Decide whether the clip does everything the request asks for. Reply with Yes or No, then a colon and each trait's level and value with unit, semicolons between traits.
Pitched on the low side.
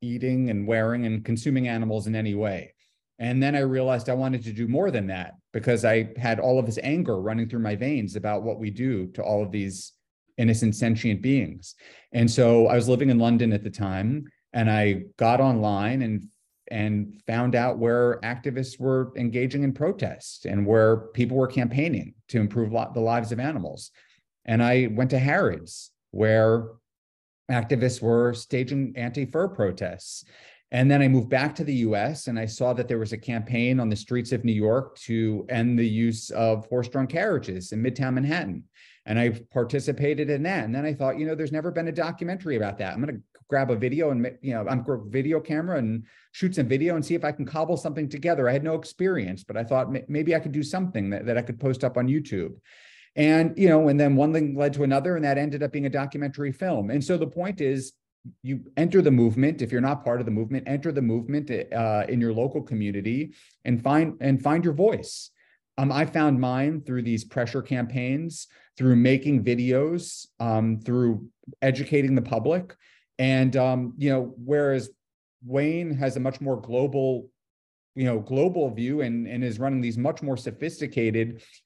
Yes: low, 125 Hz